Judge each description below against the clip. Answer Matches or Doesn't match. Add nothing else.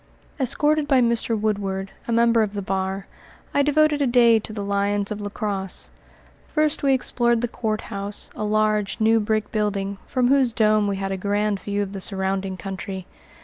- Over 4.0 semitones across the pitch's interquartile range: Doesn't match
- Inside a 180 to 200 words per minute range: Matches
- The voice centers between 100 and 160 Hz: Doesn't match